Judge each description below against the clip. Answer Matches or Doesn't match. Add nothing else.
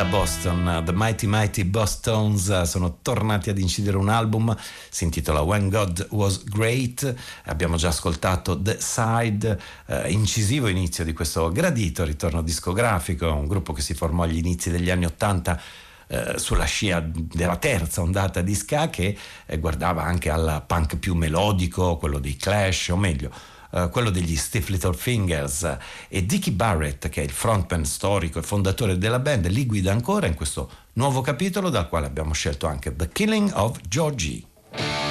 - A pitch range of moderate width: Matches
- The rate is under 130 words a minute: Doesn't match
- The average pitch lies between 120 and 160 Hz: Doesn't match